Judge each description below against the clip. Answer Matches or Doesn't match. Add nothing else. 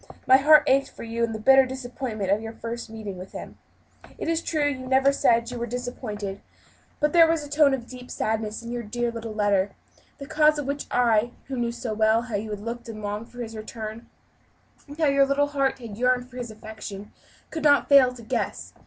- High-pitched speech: Matches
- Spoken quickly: Matches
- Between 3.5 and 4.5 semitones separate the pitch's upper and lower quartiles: Matches